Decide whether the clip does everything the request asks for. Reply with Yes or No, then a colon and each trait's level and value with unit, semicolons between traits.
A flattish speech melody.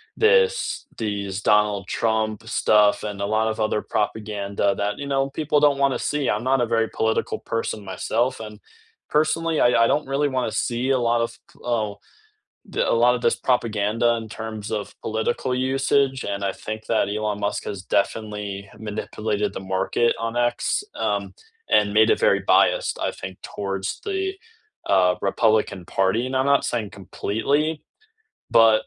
No: average, 3.8 semitones